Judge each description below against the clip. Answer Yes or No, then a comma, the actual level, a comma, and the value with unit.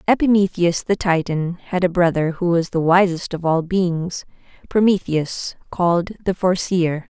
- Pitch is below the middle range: No, medium, 175 Hz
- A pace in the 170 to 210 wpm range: No, slow, 135 wpm